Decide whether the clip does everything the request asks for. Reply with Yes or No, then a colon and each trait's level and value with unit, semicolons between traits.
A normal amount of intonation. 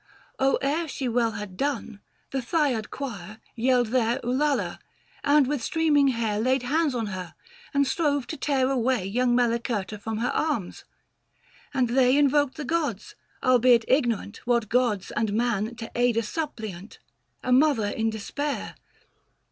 Yes: average, 3.9 semitones